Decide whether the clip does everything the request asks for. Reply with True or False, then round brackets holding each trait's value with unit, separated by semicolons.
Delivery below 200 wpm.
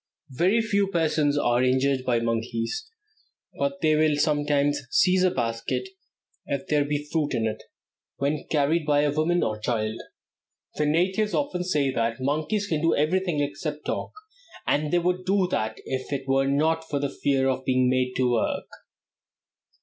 True (165 wpm)